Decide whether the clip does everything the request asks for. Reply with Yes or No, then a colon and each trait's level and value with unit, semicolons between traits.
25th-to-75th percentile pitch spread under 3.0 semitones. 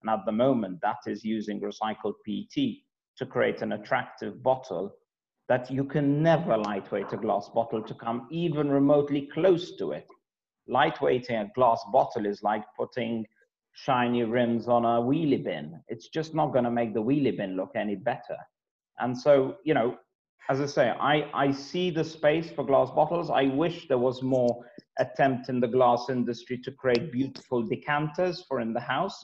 No: average, 4.0 semitones